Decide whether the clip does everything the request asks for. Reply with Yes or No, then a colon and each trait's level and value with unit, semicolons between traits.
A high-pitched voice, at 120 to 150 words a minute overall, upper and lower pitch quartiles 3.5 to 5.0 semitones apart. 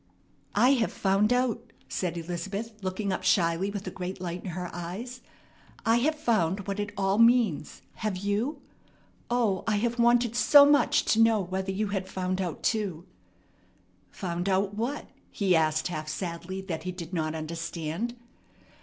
No: high, 195 Hz; average, 165 wpm; average, 4.3 semitones